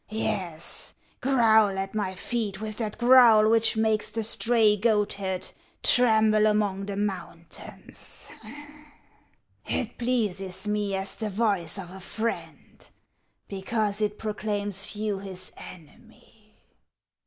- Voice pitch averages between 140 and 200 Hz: No, high, 210 Hz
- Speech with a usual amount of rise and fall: No, narrow, 2.1 semitones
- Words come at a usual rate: No, slow, 110 wpm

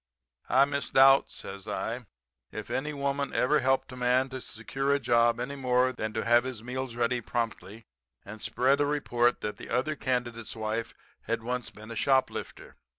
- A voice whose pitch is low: Yes, low, 125 Hz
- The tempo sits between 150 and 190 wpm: Yes, average, 175 wpm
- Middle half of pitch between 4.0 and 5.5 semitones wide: No, narrow, 2.5 semitones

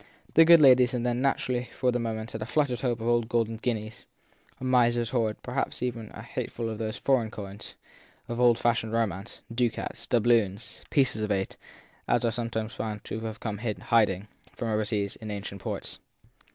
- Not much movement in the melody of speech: Yes, narrow, 2.1 semitones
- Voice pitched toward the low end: Yes, low, 115 Hz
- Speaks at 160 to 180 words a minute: No, average, 195 wpm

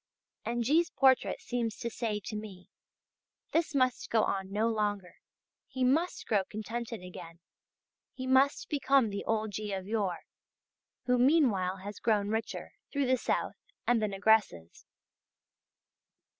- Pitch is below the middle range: No, high, 220 Hz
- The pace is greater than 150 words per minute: No, average, 140 wpm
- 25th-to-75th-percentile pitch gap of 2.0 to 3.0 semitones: No, average, 4.1 semitones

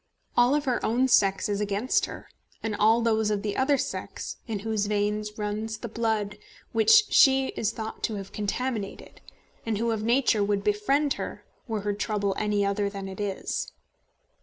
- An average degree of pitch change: No, narrow, 2.2 semitones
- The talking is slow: No, average, 175 wpm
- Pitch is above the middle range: Yes, high, 215 Hz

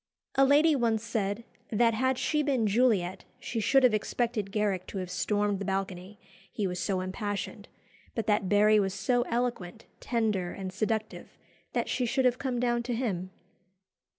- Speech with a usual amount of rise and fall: Yes, average, 3.7 semitones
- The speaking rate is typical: Yes, average, 170 wpm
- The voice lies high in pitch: Yes, high, 215 Hz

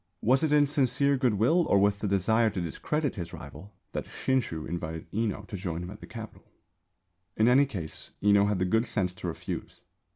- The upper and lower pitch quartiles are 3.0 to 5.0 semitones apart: No, wide, 5.6 semitones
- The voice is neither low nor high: No, low, 105 Hz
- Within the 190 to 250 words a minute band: Yes, average, 195 wpm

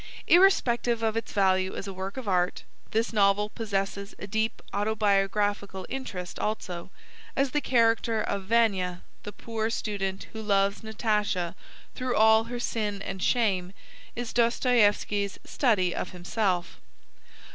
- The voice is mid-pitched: No, high, 210 Hz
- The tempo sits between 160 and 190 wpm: No, slow, 135 wpm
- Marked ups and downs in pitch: No, average, 2.8 semitones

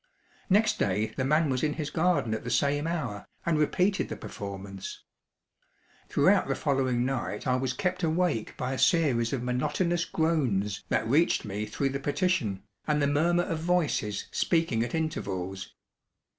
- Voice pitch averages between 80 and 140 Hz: Yes, low, 135 Hz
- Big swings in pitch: Yes, wide, 6.8 semitones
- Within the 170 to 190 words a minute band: No, average, 160 wpm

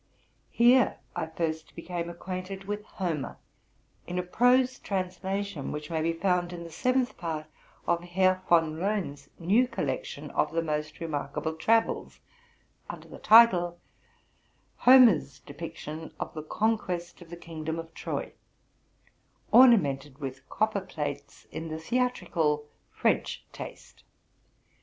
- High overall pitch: No, medium, 175 Hz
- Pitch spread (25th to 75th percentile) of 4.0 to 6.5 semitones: Yes, average, 4.3 semitones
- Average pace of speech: No, slow, 130 wpm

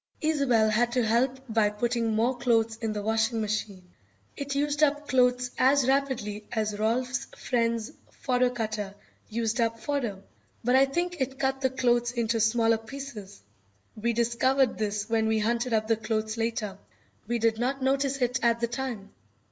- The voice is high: Yes, high, 235 Hz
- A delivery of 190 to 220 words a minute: No, average, 165 wpm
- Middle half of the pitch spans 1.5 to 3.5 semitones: Yes, average, 2.9 semitones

